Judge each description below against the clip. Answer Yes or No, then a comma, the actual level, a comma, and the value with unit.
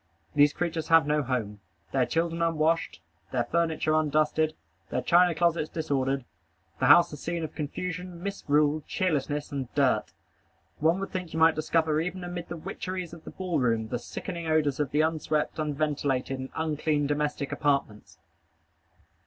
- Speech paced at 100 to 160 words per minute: Yes, average, 155 wpm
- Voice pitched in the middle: Yes, medium, 155 Hz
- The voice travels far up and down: No, average, 2.7 semitones